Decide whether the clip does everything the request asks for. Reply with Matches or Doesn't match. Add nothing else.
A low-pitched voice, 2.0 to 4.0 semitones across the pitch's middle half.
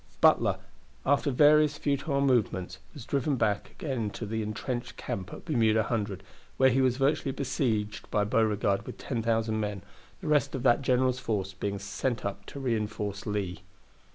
Doesn't match